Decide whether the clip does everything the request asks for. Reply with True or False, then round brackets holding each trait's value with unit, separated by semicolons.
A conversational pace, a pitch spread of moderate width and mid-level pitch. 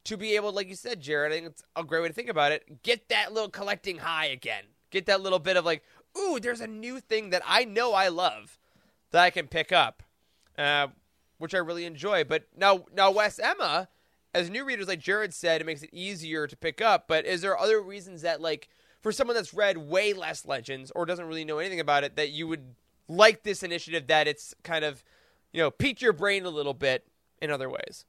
False (235 wpm; 4.4 semitones; 180 Hz)